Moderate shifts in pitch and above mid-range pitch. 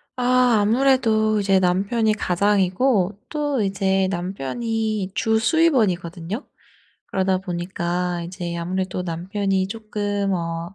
Yes: average, 3.4 semitones; high, 195 Hz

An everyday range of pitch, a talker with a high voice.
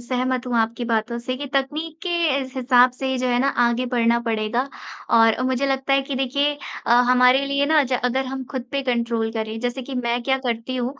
No: narrow, 2.2 semitones; very high, 255 Hz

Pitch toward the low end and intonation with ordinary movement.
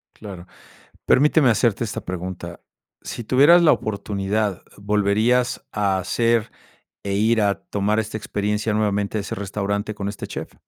No: low, 105 Hz; narrow, 2.1 semitones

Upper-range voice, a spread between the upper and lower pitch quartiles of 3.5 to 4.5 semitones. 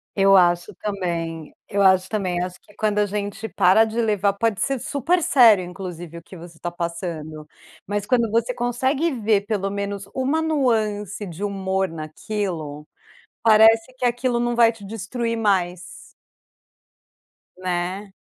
Yes: high, 200 Hz; average, 4.1 semitones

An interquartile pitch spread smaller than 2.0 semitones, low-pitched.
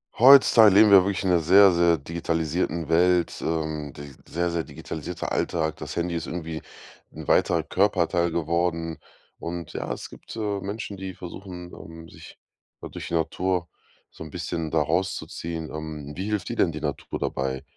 No: narrow, 2.5 semitones; very low, 85 Hz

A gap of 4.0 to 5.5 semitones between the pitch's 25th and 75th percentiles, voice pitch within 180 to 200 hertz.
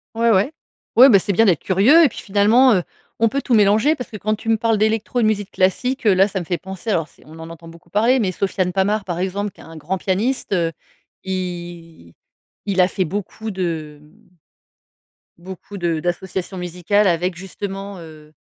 No: average, 3.6 semitones; high, 190 Hz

